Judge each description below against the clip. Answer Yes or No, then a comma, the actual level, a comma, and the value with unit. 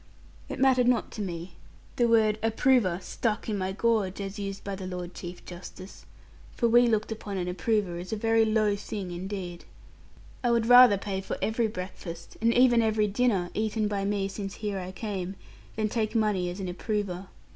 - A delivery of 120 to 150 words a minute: No, average, 190 wpm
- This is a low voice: No, high, 205 Hz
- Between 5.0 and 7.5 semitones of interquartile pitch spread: No, average, 3.2 semitones